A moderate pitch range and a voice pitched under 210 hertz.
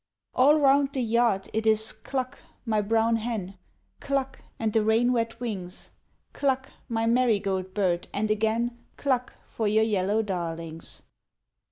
No: average, 3.2 semitones; high, 225 Hz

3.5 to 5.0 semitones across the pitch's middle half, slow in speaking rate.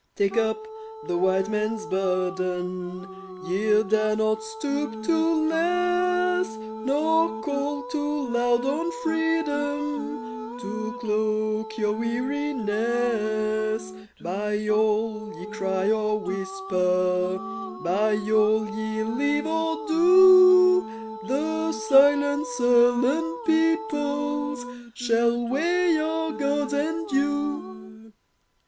No: wide, 5.5 semitones; slow, 90 wpm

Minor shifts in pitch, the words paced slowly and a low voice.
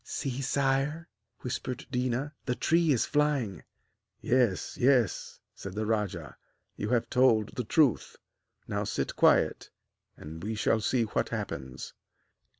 No: average, 4.3 semitones; slow, 130 wpm; low, 125 Hz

